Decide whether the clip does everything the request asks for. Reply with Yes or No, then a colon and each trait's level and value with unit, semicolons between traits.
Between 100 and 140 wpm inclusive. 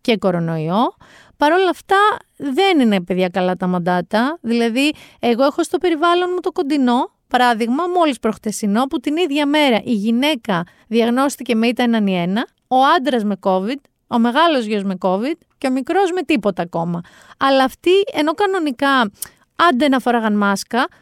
No: average, 160 wpm